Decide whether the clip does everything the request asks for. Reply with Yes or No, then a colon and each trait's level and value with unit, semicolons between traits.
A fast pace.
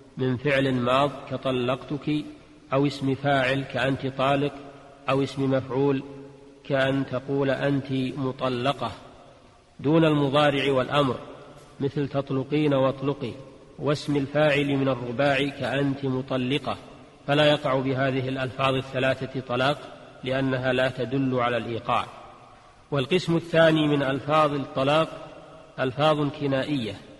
No: average, 100 wpm